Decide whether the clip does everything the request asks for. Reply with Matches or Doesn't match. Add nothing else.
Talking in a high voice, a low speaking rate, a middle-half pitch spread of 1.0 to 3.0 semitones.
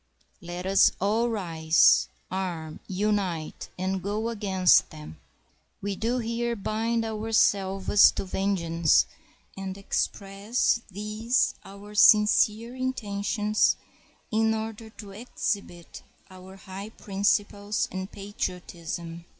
Matches